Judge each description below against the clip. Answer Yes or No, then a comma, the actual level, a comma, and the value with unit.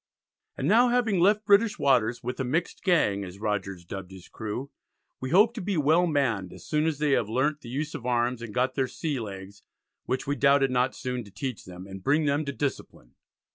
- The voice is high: No, low, 130 Hz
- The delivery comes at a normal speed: No, fast, 215 wpm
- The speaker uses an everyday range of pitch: No, wide, 5.9 semitones